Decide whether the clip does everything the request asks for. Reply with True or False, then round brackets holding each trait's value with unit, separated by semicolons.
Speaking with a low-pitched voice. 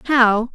False (240 Hz)